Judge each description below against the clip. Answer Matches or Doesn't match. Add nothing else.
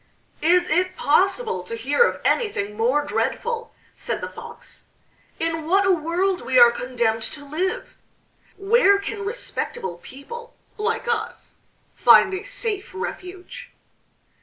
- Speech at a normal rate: Doesn't match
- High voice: Matches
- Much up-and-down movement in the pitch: Matches